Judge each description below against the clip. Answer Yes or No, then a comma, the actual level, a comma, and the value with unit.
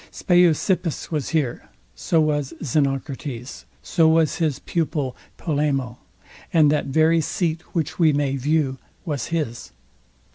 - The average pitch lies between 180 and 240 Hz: No, medium, 150 Hz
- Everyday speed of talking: No, slow, 120 wpm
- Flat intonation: No, average, 3.0 semitones